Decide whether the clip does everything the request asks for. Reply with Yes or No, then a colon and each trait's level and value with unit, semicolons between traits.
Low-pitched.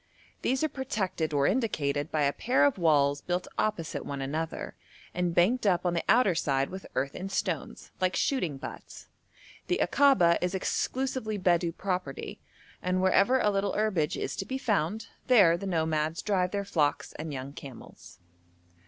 No: medium, 180 Hz